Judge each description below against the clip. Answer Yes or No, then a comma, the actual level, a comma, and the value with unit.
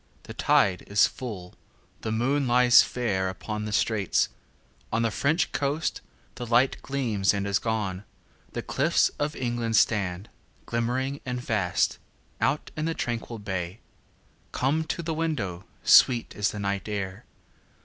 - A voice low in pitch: Yes, low, 115 Hz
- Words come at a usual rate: No, slow, 130 wpm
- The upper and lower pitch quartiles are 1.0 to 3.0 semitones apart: No, average, 4.6 semitones